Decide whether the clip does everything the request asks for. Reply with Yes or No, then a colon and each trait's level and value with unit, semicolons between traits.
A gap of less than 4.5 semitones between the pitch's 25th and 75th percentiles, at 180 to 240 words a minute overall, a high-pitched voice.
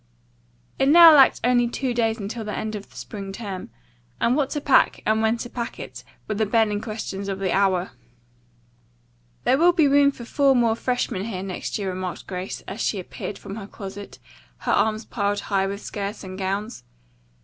Yes: average, 3.6 semitones; average, 195 wpm; high, 215 Hz